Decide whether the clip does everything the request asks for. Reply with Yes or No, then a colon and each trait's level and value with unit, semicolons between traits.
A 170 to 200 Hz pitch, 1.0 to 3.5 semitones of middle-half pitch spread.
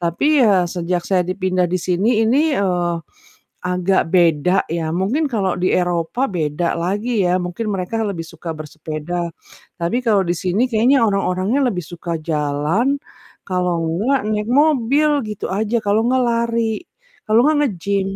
No: medium, 185 Hz; average, 4.3 semitones